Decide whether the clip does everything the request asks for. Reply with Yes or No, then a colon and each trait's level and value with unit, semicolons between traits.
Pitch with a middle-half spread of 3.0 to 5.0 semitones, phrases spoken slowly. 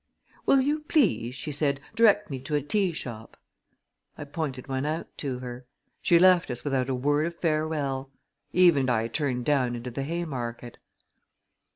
No: average, 4.7 semitones; average, 170 wpm